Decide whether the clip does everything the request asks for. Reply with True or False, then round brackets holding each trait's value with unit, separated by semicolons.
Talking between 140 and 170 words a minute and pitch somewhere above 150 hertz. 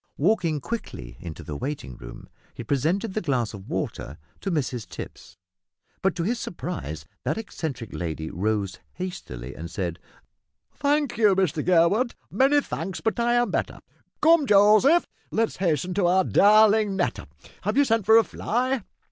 True (160 wpm; 185 Hz)